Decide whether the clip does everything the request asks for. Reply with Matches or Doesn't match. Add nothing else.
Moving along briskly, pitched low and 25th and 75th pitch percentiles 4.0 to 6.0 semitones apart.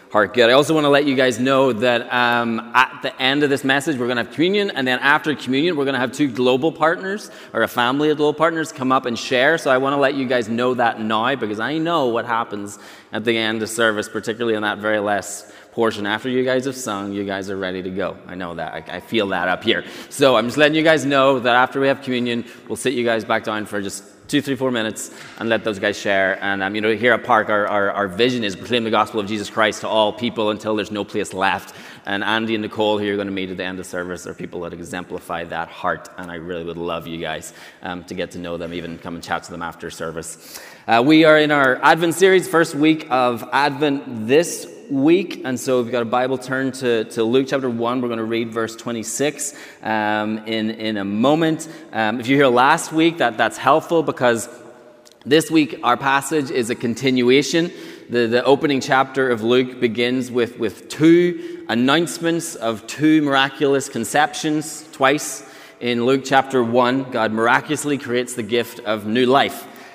Matches